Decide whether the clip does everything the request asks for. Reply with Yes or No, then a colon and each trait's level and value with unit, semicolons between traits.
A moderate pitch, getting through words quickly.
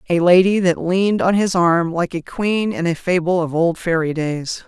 Yes: medium, 175 Hz; fast, 220 wpm